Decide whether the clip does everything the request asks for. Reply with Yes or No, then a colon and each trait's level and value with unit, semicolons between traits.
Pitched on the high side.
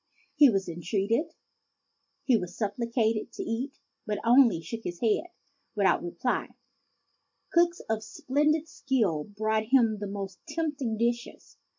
Yes: high, 225 Hz